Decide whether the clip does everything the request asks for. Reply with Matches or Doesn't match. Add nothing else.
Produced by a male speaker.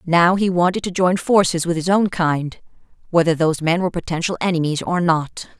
Doesn't match